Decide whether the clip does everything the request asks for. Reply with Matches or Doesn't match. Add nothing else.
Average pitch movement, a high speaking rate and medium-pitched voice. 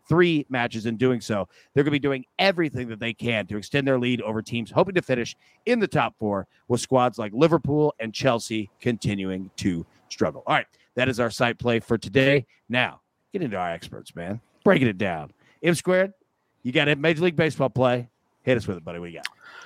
Doesn't match